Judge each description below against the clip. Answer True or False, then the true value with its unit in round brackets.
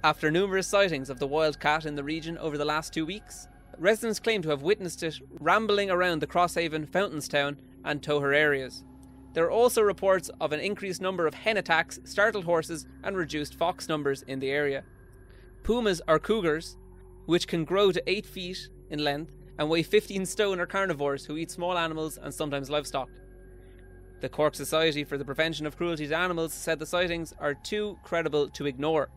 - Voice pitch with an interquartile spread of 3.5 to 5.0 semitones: True (4.1 semitones)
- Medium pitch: True (160 Hz)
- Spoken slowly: False (185 wpm)